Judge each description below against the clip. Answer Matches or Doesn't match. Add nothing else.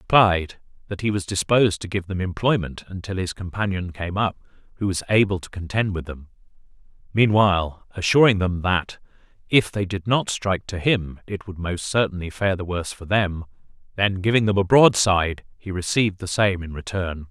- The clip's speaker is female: Doesn't match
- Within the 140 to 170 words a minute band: Doesn't match